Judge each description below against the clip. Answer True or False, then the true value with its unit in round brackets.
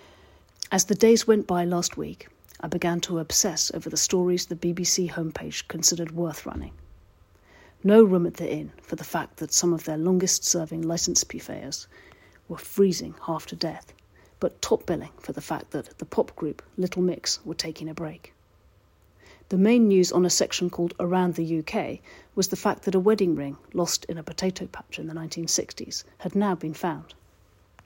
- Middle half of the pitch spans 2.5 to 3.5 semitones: True (2.8 semitones)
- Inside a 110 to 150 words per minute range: False (185 wpm)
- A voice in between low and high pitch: True (170 Hz)